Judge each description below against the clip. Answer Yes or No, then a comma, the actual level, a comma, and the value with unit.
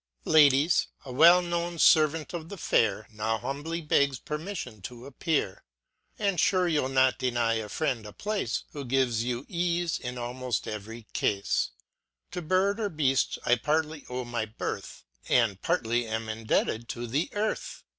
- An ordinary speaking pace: Yes, average, 155 wpm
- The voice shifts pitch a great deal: Yes, wide, 5.8 semitones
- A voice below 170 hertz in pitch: Yes, low, 135 Hz